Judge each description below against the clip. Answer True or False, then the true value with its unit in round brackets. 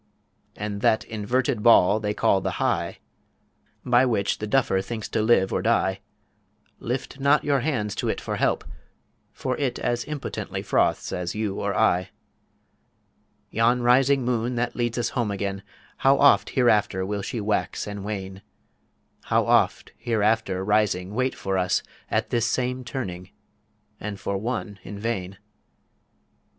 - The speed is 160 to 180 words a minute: False (150 wpm)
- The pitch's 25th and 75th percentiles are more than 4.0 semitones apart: False (3.7 semitones)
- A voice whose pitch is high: False (110 Hz)